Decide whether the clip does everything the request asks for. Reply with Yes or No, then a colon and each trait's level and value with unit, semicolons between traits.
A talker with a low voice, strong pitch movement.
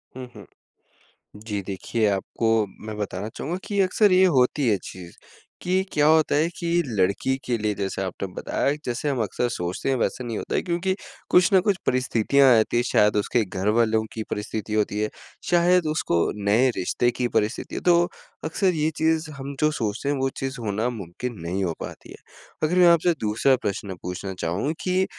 Yes: low, 120 Hz; wide, 7.1 semitones